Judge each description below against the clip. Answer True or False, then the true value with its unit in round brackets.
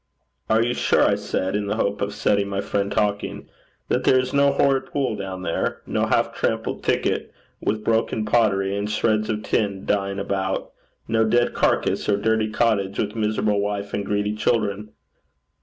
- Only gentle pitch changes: True (1.8 semitones)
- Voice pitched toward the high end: False (105 Hz)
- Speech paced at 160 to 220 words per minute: True (175 wpm)